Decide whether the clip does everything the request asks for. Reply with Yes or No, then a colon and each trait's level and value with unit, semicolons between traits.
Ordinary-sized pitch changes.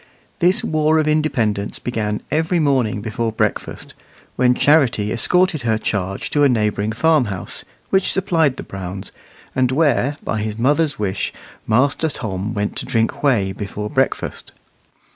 No: wide, 6.2 semitones